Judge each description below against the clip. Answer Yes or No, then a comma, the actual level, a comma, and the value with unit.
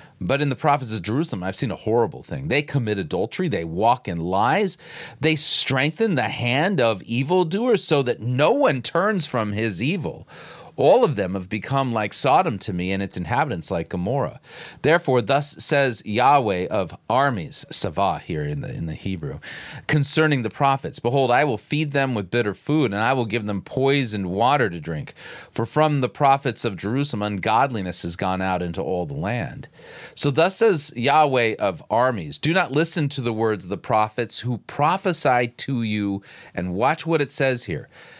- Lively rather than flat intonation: Yes, wide, 5.7 semitones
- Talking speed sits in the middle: Yes, average, 185 wpm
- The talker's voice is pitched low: Yes, low, 130 Hz